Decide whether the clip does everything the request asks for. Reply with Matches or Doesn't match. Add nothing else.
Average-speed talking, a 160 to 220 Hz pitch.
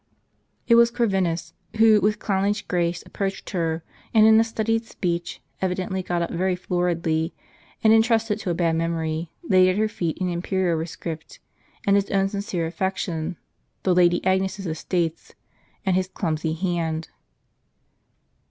Matches